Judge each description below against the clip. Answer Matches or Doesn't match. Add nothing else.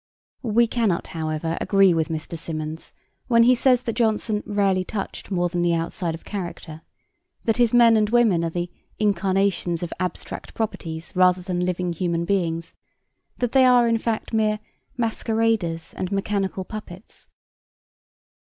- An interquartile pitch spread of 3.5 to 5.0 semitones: Matches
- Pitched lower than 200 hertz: Matches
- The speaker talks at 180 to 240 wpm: Doesn't match